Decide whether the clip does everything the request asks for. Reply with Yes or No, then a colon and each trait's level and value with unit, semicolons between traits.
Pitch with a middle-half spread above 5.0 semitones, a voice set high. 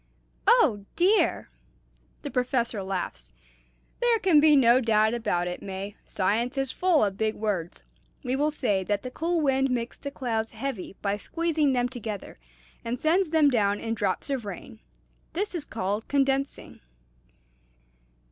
Yes: wide, 5.6 semitones; high, 245 Hz